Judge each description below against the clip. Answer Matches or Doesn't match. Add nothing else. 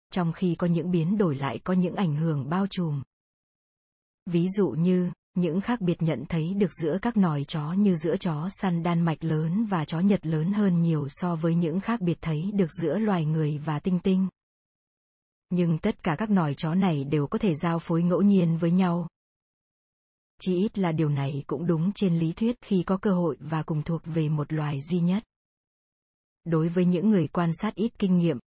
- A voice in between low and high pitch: Matches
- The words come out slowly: Doesn't match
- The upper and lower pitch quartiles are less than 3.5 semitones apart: Matches